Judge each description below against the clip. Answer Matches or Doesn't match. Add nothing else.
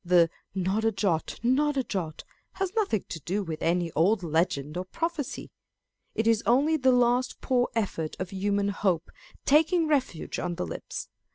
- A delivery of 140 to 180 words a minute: Matches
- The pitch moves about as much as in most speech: Doesn't match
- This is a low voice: Doesn't match